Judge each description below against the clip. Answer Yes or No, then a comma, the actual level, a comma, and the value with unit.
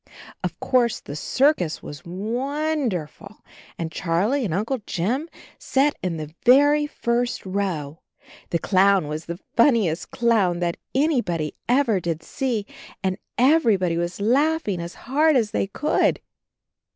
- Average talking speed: No, slow, 130 wpm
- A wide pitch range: Yes, wide, 7.5 semitones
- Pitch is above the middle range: Yes, high, 210 Hz